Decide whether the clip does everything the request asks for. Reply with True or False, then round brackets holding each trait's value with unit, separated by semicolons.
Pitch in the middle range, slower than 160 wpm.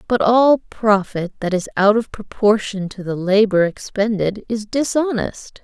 False (210 Hz; 150 wpm)